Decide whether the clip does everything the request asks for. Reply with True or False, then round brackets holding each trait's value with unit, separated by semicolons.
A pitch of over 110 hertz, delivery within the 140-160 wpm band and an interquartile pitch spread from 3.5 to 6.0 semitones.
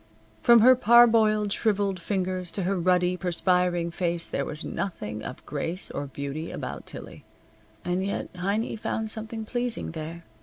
True (185 Hz; 150 wpm; 4.0 semitones)